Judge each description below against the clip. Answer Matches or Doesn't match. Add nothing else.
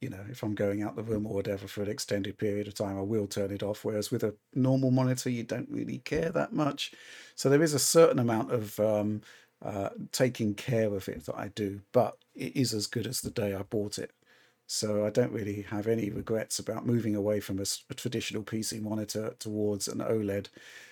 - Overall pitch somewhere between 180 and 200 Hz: Doesn't match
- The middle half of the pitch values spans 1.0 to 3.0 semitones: Matches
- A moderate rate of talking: Doesn't match